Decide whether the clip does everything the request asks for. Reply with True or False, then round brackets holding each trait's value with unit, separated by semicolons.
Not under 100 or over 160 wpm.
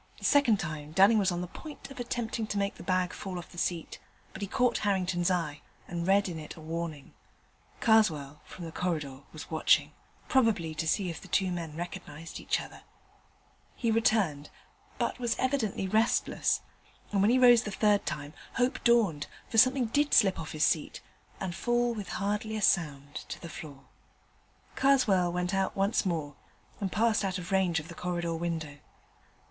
False (185 wpm)